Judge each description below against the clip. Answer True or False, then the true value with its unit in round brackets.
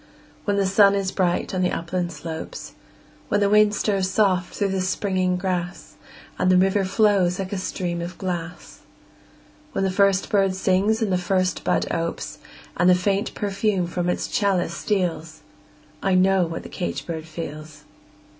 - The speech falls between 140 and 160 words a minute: False (170 wpm)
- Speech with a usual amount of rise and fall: False (2.0 semitones)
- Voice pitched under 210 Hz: True (185 Hz)